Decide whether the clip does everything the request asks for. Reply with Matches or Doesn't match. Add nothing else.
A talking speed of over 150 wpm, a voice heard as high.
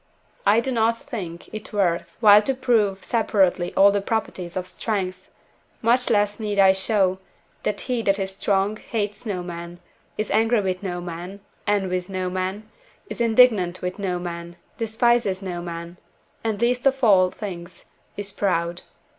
Matches